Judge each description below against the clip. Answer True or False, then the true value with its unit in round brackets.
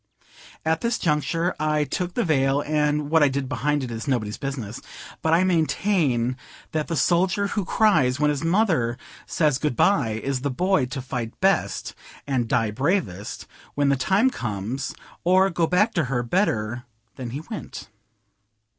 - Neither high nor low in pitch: True (150 Hz)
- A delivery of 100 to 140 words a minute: False (165 wpm)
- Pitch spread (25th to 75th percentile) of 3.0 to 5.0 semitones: False (5.5 semitones)